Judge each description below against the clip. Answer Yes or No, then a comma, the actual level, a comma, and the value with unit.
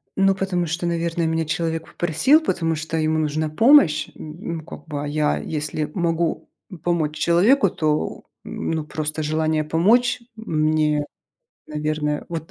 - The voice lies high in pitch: No, medium, 160 Hz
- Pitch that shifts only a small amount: Yes, narrow, 2.1 semitones